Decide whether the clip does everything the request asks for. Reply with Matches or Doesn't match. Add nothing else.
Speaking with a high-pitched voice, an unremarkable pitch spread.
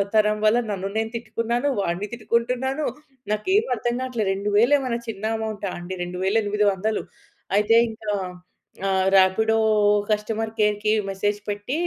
Doesn't match